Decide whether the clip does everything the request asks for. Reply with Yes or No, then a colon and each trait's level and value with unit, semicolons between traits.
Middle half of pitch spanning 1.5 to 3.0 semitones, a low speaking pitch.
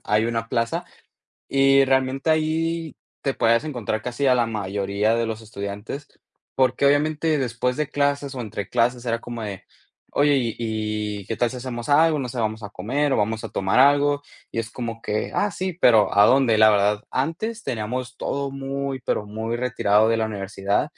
No: average, 4.2 semitones; low, 120 Hz